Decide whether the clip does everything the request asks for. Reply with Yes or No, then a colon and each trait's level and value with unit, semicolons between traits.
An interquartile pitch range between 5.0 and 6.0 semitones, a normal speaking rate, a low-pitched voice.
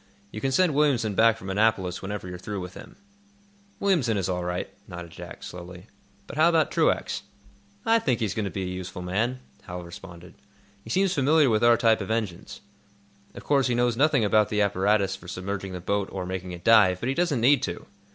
No: average, 5.3 semitones; fast, 210 wpm; low, 105 Hz